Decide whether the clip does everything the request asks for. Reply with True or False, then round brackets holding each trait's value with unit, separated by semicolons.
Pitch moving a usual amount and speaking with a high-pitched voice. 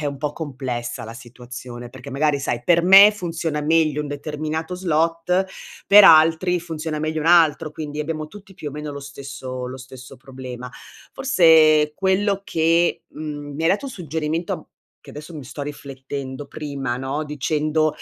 False (3.2 semitones; 150 Hz)